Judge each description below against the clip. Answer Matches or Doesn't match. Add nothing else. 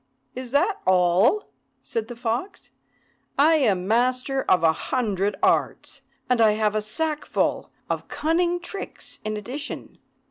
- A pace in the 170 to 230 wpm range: Doesn't match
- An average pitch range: Doesn't match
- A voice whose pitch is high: Matches